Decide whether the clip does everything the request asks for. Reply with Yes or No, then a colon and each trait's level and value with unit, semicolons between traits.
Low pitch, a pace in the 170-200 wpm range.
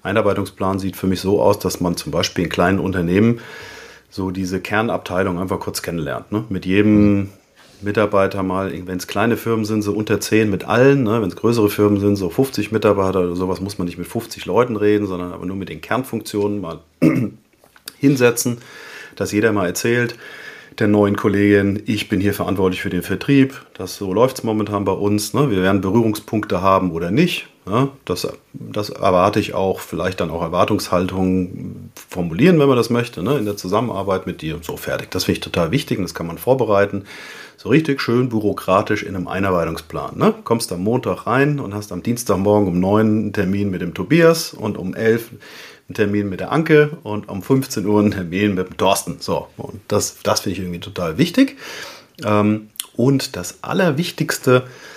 Yes: low, 105 Hz; fast, 190 wpm